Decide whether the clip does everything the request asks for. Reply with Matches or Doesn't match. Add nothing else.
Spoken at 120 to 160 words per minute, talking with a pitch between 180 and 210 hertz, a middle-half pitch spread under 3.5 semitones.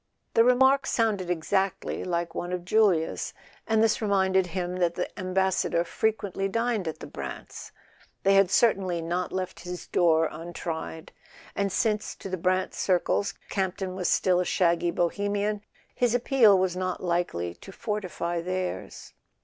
Matches